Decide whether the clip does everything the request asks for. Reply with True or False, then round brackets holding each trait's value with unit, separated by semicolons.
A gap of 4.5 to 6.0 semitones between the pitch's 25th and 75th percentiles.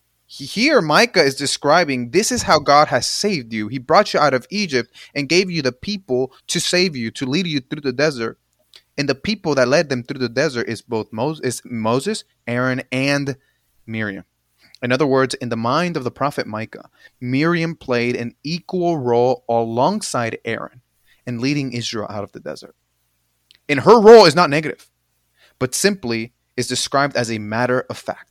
True (5.1 semitones)